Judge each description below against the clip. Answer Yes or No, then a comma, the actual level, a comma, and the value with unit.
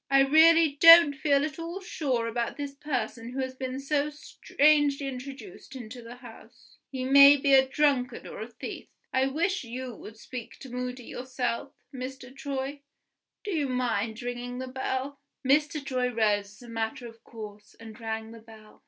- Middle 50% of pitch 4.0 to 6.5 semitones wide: No, average, 3.1 semitones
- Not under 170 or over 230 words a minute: Yes, average, 175 wpm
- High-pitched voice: Yes, very high, 260 Hz